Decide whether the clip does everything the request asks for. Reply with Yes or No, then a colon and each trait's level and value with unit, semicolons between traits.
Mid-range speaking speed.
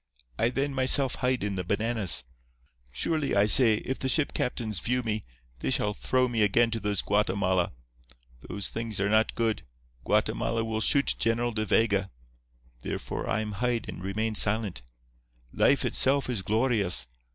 Yes: average, 160 wpm